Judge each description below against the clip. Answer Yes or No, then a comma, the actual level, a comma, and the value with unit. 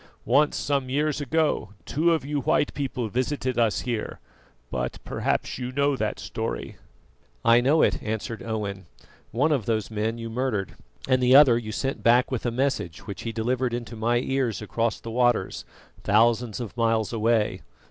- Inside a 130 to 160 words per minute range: No, average, 170 wpm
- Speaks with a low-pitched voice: Yes, low, 120 Hz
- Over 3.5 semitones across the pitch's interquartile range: No, average, 3.1 semitones